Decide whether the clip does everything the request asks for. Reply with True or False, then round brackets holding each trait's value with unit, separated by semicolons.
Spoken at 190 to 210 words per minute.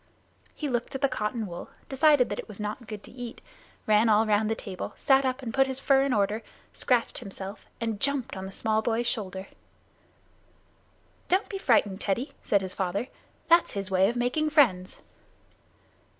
False (180 wpm)